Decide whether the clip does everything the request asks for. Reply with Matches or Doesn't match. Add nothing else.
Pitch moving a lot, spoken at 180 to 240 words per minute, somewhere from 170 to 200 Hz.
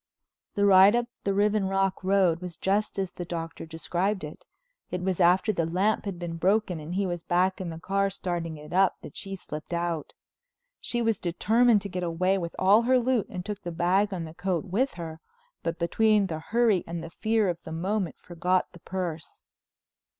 Doesn't match